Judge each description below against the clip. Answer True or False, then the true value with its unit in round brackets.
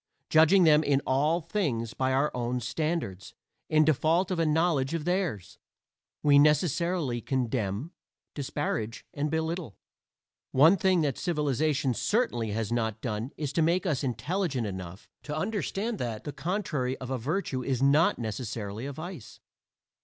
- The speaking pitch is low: False (145 Hz)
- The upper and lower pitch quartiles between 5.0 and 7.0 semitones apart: True (5.5 semitones)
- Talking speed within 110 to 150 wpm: True (145 wpm)